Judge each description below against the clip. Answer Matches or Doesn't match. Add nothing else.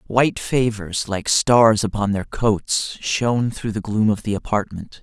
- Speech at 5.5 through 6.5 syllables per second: Doesn't match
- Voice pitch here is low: Matches